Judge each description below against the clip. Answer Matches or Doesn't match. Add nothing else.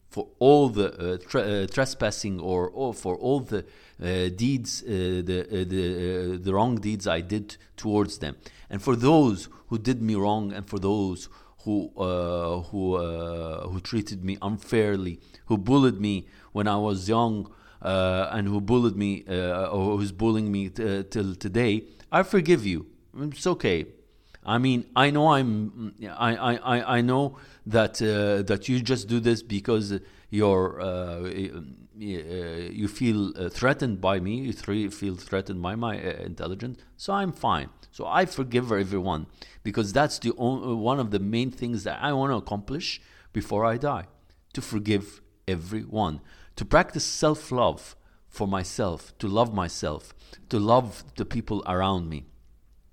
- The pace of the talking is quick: Doesn't match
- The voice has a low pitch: Matches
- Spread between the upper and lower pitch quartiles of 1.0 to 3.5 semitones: Doesn't match